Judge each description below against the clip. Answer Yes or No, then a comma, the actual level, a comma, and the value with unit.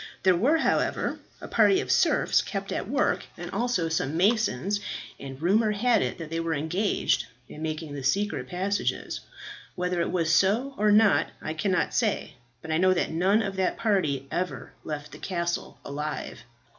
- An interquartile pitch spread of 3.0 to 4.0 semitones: No, average, 4.6 semitones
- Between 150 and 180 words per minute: Yes, average, 175 wpm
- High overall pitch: No, medium, 180 Hz